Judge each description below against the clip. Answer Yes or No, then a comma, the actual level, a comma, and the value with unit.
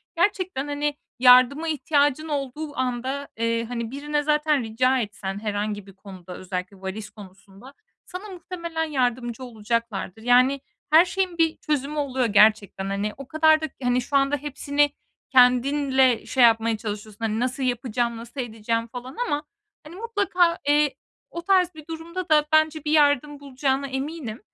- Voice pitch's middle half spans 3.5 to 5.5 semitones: Yes, average, 4.8 semitones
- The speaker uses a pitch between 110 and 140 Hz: No, very high, 265 Hz